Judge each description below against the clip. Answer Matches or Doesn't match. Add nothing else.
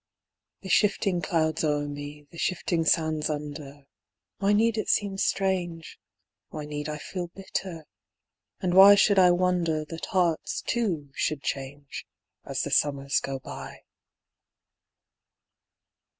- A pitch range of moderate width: Matches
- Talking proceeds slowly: Matches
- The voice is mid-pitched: Matches